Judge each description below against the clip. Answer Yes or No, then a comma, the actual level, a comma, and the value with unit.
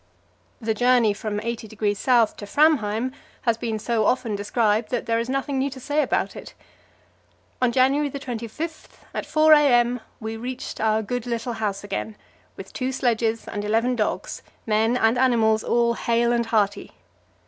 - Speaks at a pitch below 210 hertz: No, high, 235 Hz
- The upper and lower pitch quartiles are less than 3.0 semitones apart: Yes, narrow, 2.5 semitones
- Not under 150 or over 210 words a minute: Yes, average, 160 wpm